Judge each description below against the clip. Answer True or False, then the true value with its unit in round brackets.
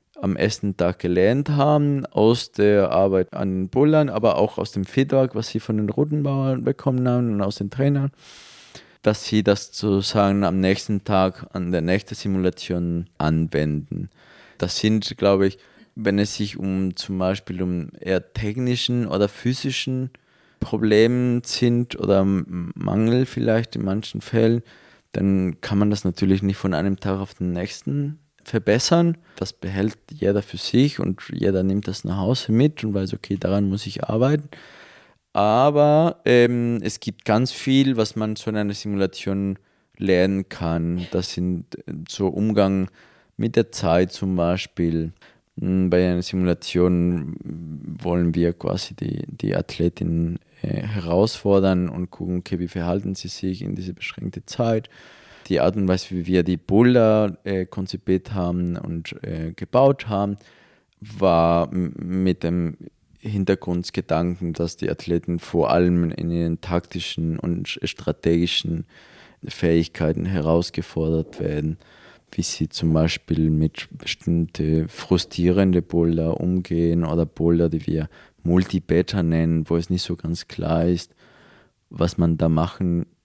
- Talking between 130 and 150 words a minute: True (145 wpm)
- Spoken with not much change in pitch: False (3.9 semitones)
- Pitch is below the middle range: True (95 Hz)